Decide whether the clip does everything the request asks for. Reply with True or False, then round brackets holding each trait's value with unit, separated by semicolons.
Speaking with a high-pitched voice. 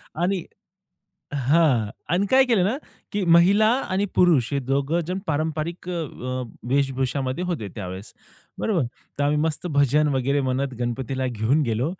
False (145 Hz)